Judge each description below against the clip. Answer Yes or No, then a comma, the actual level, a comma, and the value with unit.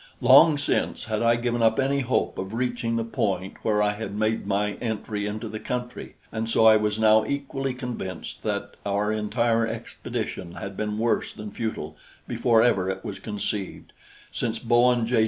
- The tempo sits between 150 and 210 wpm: Yes, average, 175 wpm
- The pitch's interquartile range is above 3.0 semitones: No, narrow, 2.4 semitones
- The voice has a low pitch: Yes, low, 110 Hz